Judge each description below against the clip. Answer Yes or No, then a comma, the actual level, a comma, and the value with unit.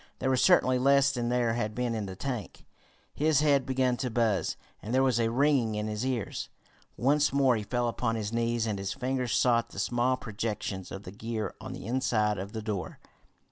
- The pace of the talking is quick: Yes, fast, 210 wpm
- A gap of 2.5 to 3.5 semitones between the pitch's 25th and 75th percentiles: Yes, average, 3.2 semitones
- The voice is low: Yes, low, 120 Hz